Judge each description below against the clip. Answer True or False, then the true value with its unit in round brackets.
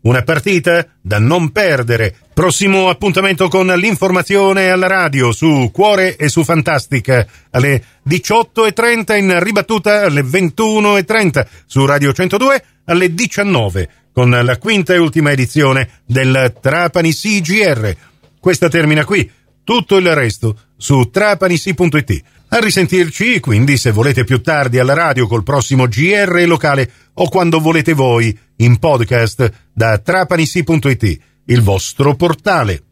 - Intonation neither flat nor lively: False (6.8 semitones)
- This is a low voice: False (160 Hz)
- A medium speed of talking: True (125 wpm)